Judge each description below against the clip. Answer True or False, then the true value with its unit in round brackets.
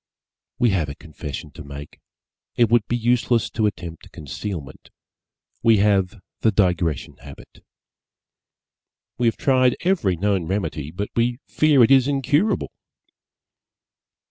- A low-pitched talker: True (105 Hz)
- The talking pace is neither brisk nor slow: False (125 wpm)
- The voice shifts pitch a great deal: True (6.5 semitones)